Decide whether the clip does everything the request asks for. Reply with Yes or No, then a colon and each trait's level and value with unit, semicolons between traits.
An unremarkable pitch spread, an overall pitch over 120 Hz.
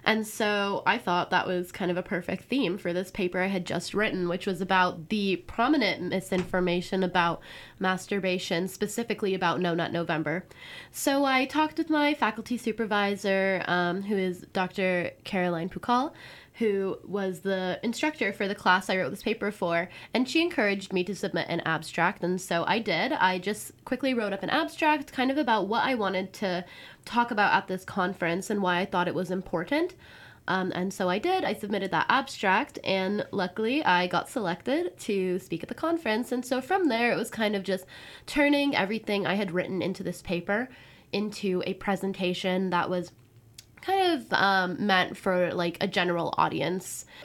Yes: average, 3.4 semitones; high, 190 Hz